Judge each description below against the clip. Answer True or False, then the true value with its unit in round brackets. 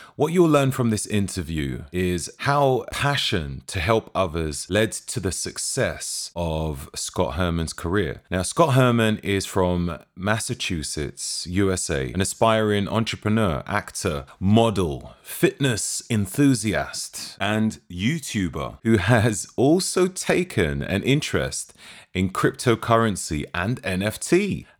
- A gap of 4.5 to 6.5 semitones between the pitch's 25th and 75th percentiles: True (5.2 semitones)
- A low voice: True (105 Hz)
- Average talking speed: False (110 wpm)